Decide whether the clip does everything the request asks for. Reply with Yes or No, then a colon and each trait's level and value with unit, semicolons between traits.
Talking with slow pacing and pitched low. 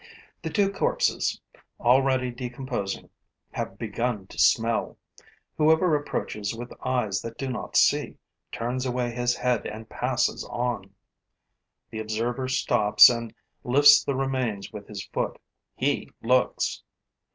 Yes: slow, 125 wpm; low, 120 Hz